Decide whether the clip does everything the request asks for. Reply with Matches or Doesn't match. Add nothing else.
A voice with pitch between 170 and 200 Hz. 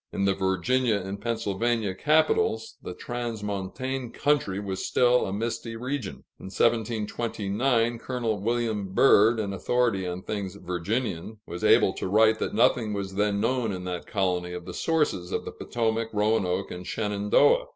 Doesn't match